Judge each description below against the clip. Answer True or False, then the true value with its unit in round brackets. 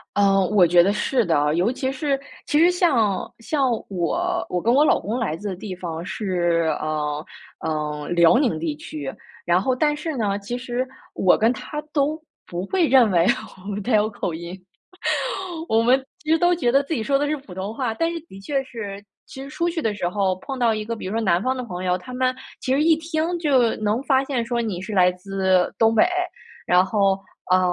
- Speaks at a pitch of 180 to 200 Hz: False (220 Hz)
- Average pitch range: False (6.8 semitones)